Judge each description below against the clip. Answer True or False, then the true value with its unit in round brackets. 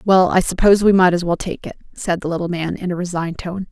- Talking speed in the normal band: False (275 wpm)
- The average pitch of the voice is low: False (180 Hz)